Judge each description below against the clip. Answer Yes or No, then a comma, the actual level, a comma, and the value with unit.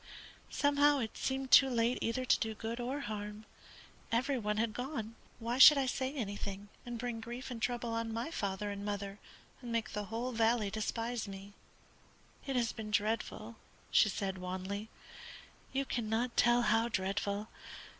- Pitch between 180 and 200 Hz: No, high, 230 Hz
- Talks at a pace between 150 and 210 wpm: Yes, average, 165 wpm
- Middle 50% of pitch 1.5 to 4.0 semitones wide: Yes, average, 2.8 semitones